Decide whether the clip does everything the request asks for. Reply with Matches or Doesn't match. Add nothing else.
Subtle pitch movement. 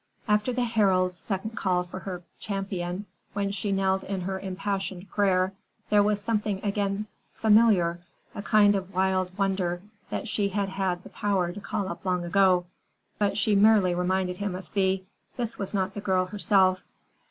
Matches